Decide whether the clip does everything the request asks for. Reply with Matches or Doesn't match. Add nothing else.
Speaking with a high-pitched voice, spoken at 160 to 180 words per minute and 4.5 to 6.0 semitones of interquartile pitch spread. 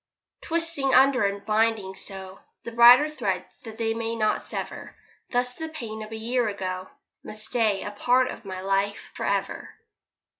Doesn't match